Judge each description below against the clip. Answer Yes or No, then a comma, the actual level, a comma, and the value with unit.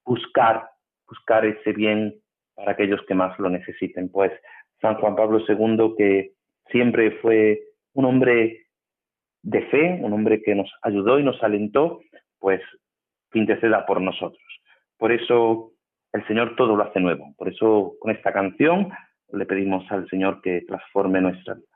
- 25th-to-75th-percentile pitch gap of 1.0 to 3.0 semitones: Yes, narrow, 2.6 semitones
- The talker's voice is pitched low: Yes, low, 105 Hz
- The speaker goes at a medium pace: Yes, average, 150 wpm